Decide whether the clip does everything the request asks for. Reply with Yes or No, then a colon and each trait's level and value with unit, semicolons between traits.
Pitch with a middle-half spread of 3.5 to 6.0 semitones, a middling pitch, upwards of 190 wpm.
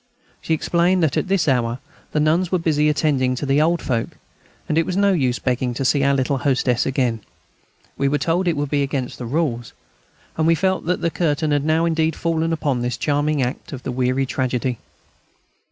Yes: average, 4.1 semitones; medium, 145 Hz; fast, 205 wpm